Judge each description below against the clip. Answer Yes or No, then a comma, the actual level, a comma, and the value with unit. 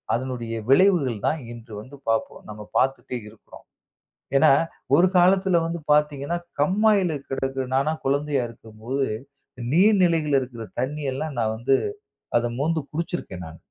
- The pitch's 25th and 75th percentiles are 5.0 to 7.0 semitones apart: Yes, wide, 5.4 semitones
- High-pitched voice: No, low, 135 Hz